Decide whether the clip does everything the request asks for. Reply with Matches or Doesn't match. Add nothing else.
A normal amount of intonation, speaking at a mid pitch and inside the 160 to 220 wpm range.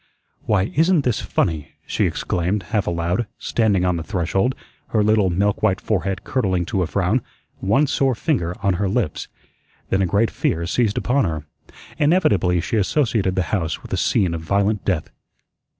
Doesn't match